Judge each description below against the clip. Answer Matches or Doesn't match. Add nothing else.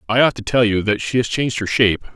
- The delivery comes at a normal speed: Doesn't match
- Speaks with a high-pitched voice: Doesn't match